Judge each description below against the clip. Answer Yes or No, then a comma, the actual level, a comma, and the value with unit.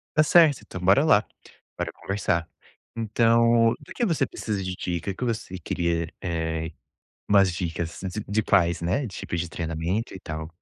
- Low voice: Yes, very low, 95 Hz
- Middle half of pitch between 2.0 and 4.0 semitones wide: No, average, 5.1 semitones